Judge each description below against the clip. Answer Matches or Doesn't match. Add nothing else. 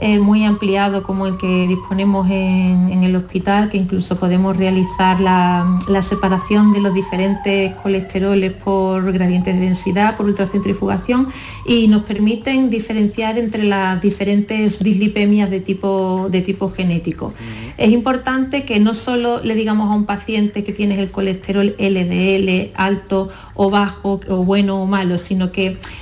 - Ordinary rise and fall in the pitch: Doesn't match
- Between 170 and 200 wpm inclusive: Doesn't match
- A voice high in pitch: Matches